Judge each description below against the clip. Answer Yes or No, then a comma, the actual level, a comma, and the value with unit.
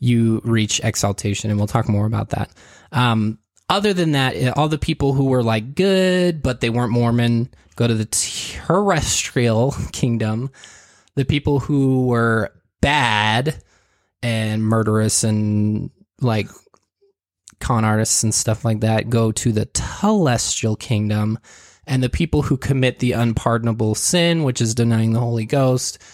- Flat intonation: No, average, 3.3 semitones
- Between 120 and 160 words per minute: Yes, average, 145 wpm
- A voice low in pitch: Yes, low, 115 Hz